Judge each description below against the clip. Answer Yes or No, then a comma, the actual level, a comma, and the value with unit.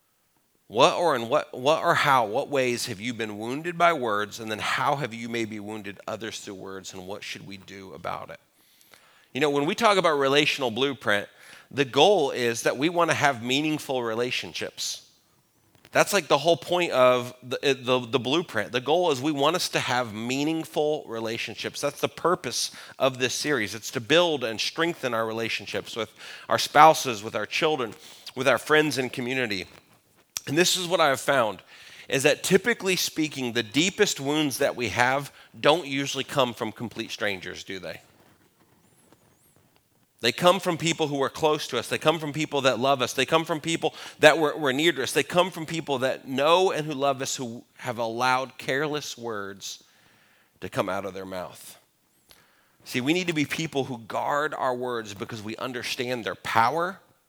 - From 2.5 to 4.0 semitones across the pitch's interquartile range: No, average, 4.8 semitones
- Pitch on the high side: No, low, 135 Hz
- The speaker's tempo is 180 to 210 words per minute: Yes, average, 190 wpm